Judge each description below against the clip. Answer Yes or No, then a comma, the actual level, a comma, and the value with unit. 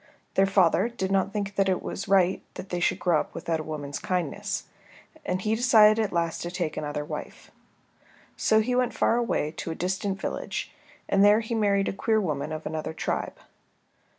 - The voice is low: No, high, 190 Hz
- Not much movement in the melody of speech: No, average, 4.0 semitones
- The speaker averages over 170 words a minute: Yes, average, 190 wpm